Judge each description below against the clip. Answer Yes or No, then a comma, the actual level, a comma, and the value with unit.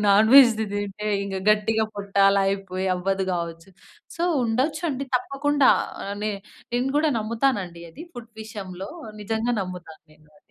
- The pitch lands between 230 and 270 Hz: No, high, 215 Hz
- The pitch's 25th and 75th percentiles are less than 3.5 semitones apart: No, average, 4.1 semitones